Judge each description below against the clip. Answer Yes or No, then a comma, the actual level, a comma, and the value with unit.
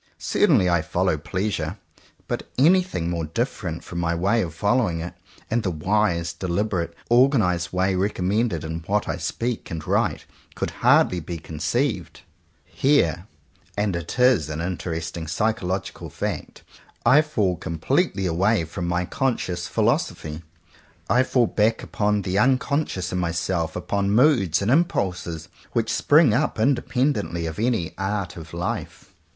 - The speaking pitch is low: Yes, very low, 95 Hz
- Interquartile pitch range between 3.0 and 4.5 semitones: No, average, 5.1 semitones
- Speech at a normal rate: Yes, average, 150 wpm